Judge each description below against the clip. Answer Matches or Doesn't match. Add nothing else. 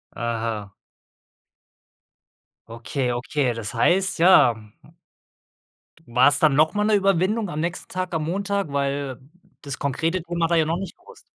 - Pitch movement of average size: Doesn't match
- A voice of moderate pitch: Matches